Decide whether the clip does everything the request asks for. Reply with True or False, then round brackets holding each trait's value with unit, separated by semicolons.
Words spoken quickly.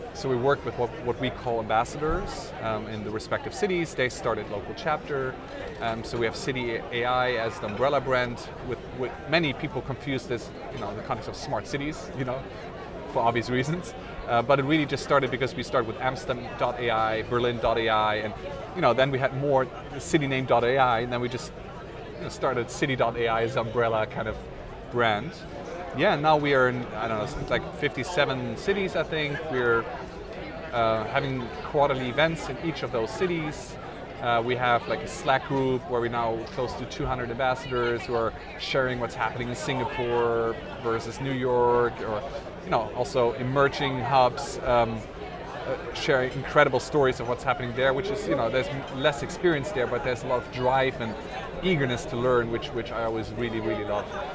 False (185 wpm)